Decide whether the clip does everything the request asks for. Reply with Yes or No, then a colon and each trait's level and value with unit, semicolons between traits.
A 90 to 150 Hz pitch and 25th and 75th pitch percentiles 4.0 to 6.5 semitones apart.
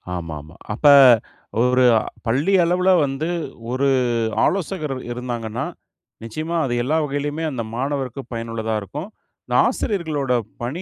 Yes: low, 135 Hz; average, 5.0 semitones